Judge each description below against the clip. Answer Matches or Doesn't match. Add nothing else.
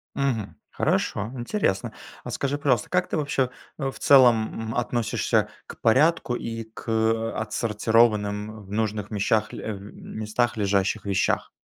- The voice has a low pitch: Matches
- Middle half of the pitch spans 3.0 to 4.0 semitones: Doesn't match